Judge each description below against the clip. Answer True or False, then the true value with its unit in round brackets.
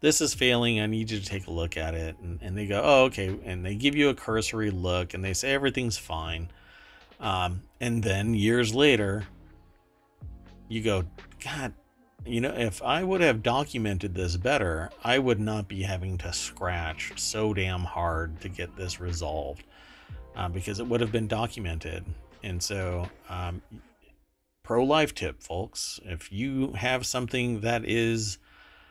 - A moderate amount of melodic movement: True (4.6 semitones)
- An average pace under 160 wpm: False (170 wpm)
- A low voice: True (100 Hz)